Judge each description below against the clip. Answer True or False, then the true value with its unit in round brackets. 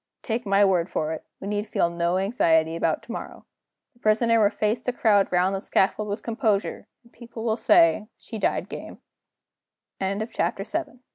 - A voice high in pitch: True (205 Hz)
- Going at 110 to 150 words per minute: False (165 wpm)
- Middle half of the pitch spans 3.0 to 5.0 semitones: True (3.9 semitones)